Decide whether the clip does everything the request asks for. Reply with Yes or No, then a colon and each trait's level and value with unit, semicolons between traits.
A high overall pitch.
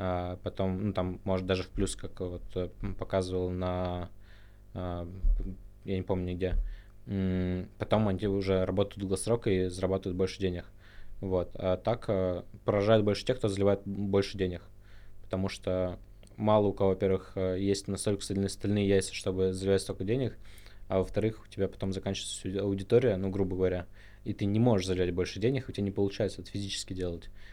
No: very low, 95 Hz